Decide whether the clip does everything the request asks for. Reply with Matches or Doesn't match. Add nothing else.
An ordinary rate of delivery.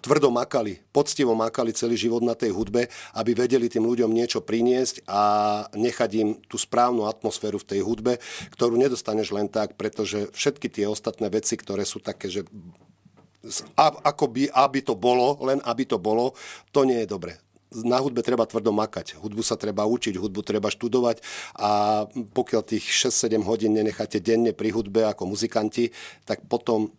Doesn't match